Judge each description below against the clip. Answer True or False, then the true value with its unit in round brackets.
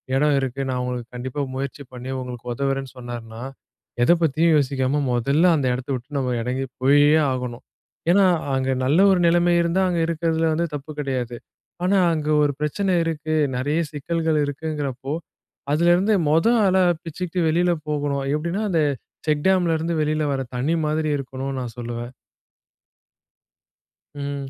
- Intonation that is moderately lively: True (3.9 semitones)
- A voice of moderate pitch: True (145 Hz)